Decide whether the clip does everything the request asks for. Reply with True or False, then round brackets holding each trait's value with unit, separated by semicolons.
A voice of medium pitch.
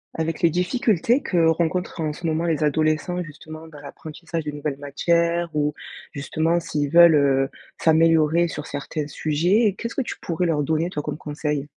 True (160 Hz)